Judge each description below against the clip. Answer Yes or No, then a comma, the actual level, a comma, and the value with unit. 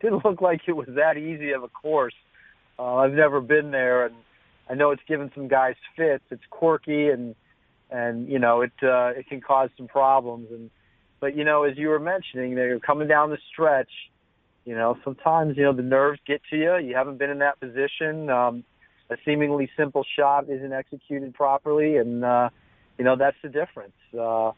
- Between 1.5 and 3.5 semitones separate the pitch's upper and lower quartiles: Yes, average, 3.2 semitones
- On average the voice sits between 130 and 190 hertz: Yes, low, 135 Hz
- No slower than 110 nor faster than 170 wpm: No, average, 200 wpm